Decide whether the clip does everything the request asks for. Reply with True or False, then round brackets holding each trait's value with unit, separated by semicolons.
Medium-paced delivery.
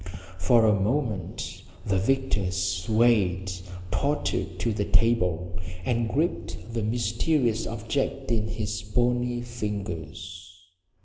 False (105 wpm)